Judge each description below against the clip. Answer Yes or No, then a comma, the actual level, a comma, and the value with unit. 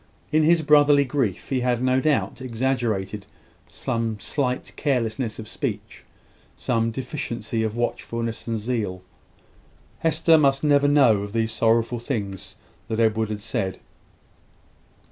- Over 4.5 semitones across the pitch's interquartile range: No, average, 3.7 semitones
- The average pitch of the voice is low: Yes, low, 115 Hz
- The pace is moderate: No, slow, 125 wpm